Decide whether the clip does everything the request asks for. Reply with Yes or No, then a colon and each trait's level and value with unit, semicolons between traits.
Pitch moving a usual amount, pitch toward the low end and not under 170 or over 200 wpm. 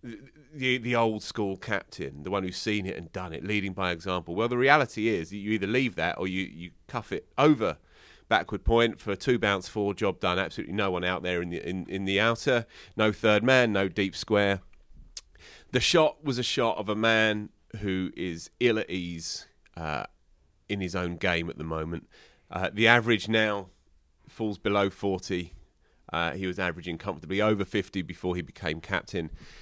Yes: average, 3.7 semitones; low, 100 Hz; average, 190 wpm